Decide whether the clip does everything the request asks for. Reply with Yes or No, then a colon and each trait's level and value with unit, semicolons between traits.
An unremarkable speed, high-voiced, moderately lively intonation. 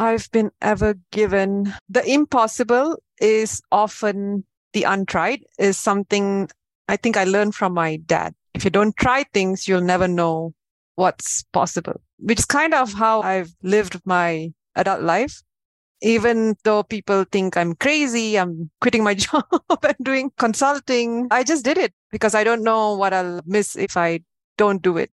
Yes: average, 160 wpm; high, 210 Hz; average, 3.6 semitones